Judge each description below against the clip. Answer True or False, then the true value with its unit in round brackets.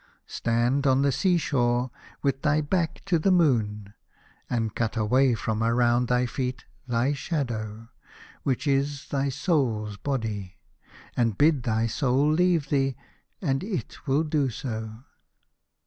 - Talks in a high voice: False (130 Hz)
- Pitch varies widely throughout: False (4.0 semitones)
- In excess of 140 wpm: False (135 wpm)